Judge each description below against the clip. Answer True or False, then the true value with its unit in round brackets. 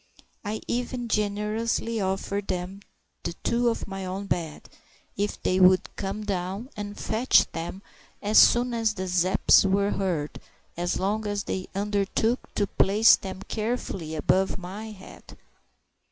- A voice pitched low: False (200 Hz)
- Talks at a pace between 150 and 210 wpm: False (140 wpm)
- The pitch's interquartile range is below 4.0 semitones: True (2.4 semitones)